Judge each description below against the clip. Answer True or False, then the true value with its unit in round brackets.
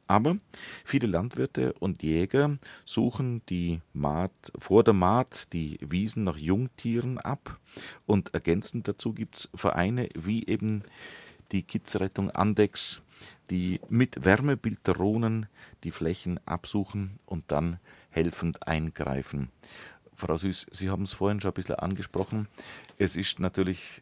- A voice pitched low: True (95 Hz)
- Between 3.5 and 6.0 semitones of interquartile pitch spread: True (4.5 semitones)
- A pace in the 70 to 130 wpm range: True (125 wpm)